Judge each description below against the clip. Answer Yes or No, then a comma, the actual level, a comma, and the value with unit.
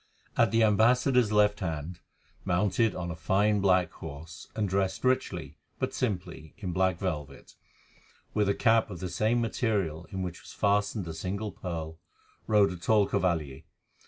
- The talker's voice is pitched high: No, very low, 95 Hz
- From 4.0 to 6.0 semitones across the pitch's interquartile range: No, average, 3.6 semitones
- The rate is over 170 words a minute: No, average, 160 wpm